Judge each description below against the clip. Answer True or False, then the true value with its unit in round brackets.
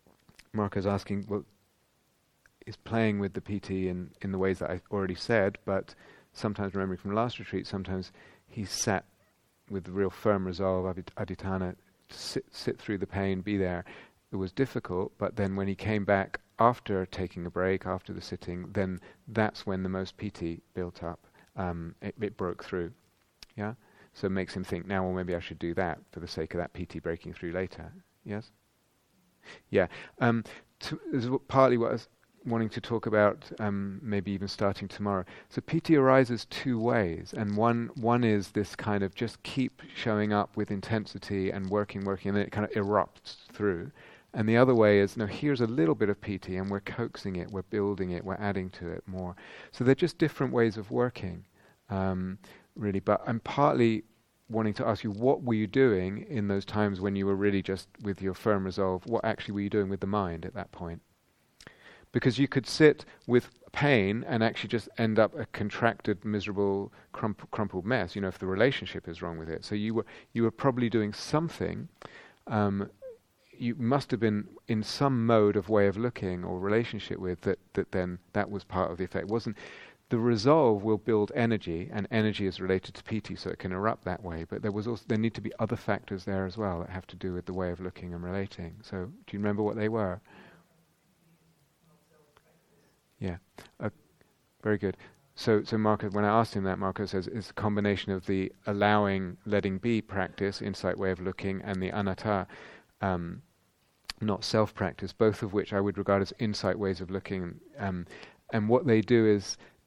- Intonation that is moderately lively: True (3.0 semitones)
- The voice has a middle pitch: False (100 Hz)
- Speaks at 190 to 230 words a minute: True (205 wpm)